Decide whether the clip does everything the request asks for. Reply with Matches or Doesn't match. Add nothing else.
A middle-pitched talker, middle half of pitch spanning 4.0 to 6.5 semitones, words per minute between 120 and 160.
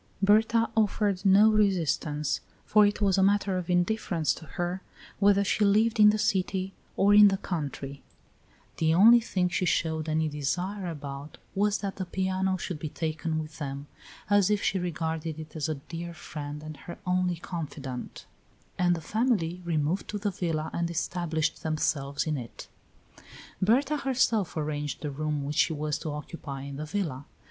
Doesn't match